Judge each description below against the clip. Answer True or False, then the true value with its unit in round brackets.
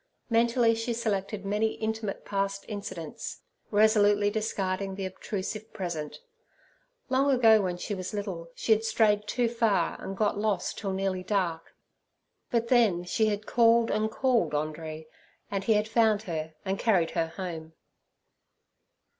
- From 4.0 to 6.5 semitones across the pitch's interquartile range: False (3.0 semitones)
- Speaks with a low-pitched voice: False (205 Hz)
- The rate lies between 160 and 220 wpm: False (145 wpm)